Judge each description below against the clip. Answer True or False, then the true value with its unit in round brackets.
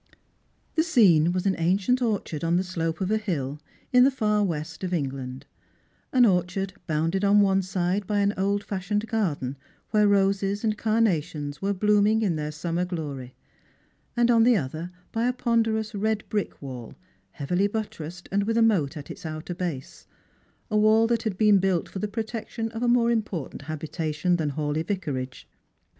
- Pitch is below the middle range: False (190 Hz)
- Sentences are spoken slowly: False (180 wpm)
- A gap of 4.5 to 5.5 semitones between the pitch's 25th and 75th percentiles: True (5.2 semitones)